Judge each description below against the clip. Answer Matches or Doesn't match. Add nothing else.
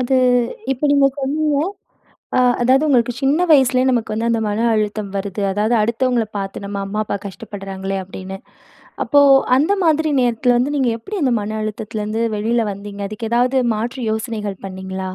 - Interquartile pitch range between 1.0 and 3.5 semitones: Doesn't match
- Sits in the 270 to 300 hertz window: Doesn't match